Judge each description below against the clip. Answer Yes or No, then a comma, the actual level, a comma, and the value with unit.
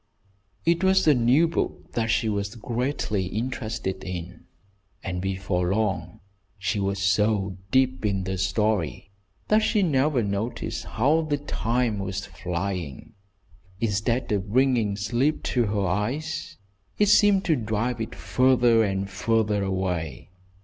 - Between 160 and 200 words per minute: No, slow, 135 wpm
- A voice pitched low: Yes, low, 110 Hz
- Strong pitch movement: No, average, 4.8 semitones